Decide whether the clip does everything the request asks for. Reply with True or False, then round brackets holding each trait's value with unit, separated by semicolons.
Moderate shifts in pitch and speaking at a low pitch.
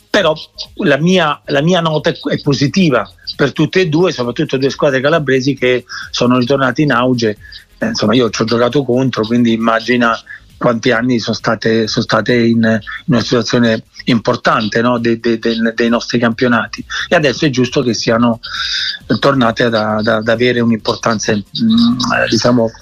True (3.4 semitones; 120 Hz)